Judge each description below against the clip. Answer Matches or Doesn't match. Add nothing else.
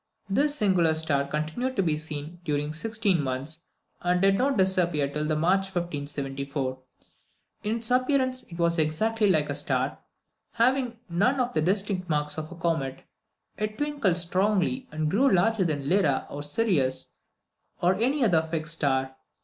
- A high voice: Doesn't match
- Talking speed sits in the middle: Matches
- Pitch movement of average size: Doesn't match